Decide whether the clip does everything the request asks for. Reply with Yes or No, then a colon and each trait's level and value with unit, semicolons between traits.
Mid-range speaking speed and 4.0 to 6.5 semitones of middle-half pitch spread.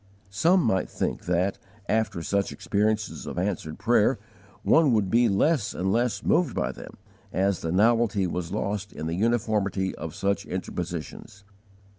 No: average, 150 wpm; average, 3.2 semitones